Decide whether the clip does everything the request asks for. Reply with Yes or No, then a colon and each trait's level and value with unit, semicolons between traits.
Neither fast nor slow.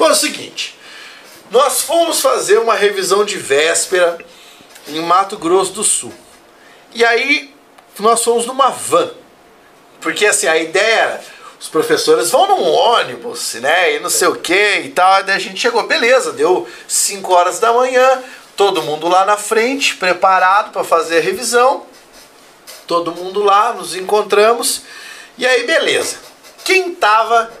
Yes: average, 150 wpm